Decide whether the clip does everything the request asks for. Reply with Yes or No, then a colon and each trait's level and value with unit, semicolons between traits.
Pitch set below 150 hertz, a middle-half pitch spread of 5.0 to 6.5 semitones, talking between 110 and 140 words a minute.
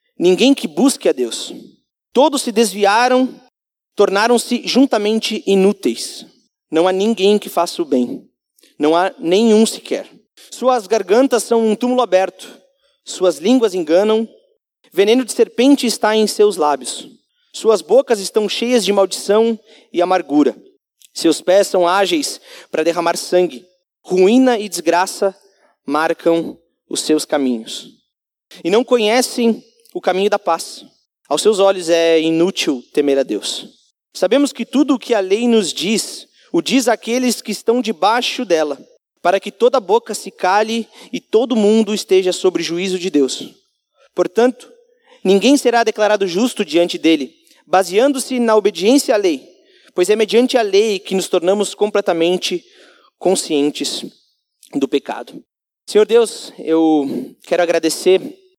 No: high, 210 Hz; wide, 5.6 semitones; average, 135 wpm